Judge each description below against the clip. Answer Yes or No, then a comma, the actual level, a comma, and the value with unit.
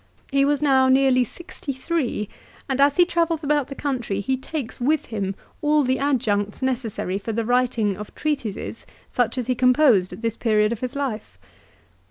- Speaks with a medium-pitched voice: No, very high, 255 Hz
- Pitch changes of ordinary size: Yes, average, 4.1 semitones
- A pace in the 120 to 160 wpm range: No, average, 180 wpm